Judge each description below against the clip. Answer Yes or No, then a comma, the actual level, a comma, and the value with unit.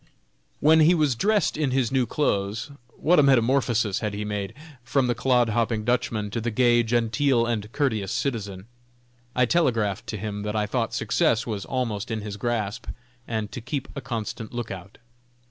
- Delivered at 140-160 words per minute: No, average, 175 wpm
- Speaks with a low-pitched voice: Yes, low, 115 Hz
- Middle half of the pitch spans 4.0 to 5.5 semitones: No, average, 3.4 semitones